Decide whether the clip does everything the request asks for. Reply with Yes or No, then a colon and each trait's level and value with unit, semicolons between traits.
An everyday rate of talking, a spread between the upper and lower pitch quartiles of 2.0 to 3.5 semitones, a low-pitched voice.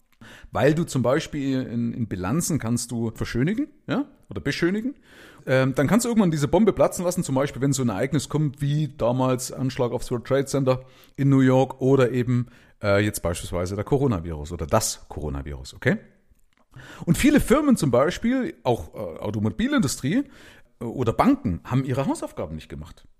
No: average, 170 wpm; average, 5.1 semitones; low, 130 Hz